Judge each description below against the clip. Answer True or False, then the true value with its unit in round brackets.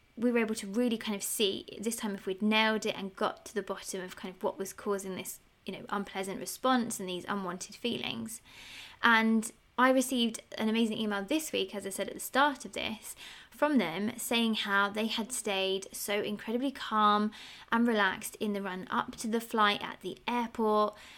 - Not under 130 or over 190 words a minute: False (205 wpm)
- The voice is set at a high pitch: True (215 Hz)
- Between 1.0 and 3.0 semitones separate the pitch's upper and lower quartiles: True (2.7 semitones)